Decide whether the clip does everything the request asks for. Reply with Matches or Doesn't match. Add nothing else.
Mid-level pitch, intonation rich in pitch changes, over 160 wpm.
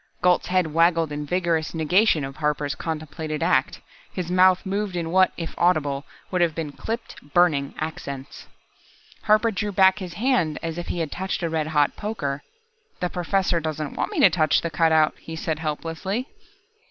Doesn't match